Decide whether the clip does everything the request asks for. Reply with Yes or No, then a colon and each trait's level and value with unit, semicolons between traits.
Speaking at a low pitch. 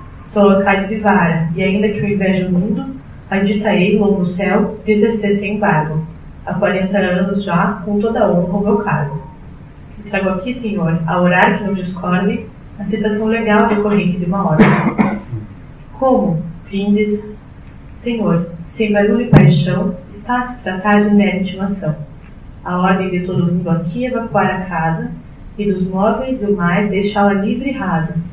No: high, 195 Hz